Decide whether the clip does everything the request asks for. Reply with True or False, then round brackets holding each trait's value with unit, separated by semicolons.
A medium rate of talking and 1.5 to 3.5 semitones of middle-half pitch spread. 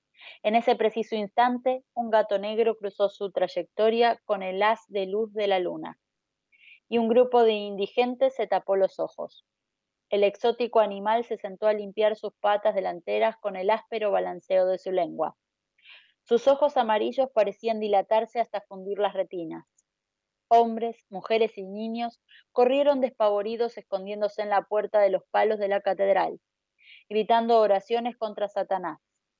True (150 wpm; 2.6 semitones)